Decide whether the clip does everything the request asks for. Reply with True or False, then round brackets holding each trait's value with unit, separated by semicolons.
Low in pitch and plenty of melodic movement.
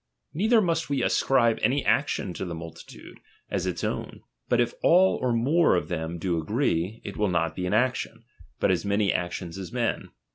True (105 Hz; 7.3 semitones)